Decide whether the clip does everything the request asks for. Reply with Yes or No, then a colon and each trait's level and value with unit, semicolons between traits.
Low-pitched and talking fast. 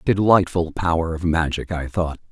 No: very low, 85 Hz; average, 155 wpm